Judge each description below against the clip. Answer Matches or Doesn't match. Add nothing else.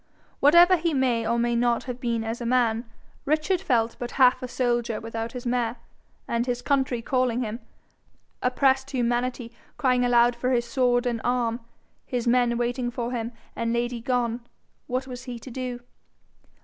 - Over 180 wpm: Doesn't match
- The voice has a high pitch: Matches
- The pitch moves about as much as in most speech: Doesn't match